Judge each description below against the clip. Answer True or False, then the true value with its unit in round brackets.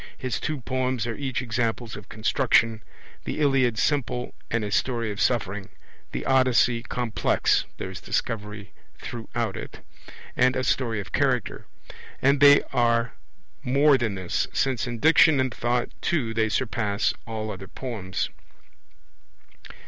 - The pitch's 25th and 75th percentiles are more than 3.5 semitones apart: False (2.9 semitones)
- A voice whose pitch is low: True (120 Hz)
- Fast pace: False (140 wpm)